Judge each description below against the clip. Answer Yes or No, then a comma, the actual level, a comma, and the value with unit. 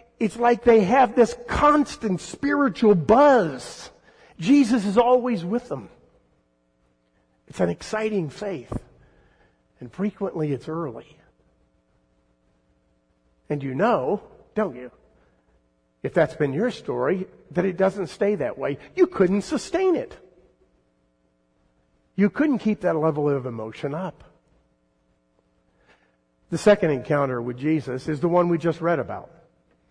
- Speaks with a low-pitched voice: No, medium, 155 Hz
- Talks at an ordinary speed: No, slow, 120 wpm